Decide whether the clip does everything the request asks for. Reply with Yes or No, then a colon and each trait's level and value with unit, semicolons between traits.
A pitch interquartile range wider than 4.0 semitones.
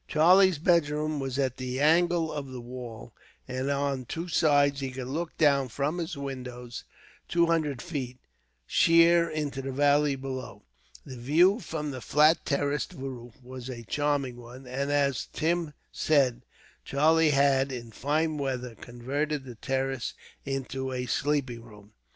No: average, 3.0 semitones